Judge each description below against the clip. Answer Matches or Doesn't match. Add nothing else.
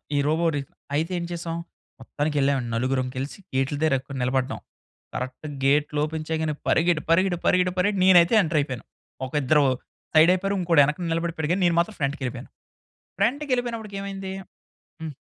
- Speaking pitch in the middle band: Matches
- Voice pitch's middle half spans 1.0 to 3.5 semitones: Doesn't match